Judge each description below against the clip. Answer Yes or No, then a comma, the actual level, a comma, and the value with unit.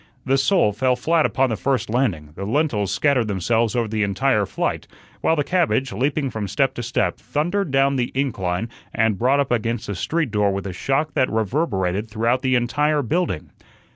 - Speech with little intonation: No, average, 4.8 semitones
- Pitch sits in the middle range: No, low, 120 Hz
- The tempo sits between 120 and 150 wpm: No, average, 190 wpm